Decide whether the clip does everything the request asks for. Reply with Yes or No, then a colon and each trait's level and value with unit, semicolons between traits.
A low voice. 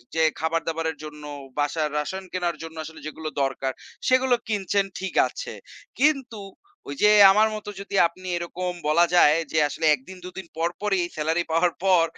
No: medium, 170 Hz